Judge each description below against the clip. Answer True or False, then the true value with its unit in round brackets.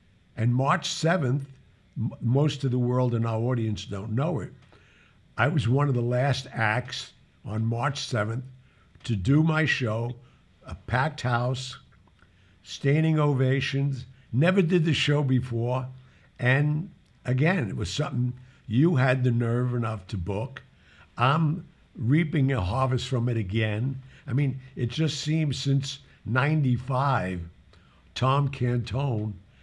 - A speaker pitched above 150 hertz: False (130 Hz)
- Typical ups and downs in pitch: True (3.3 semitones)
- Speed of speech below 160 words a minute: True (135 wpm)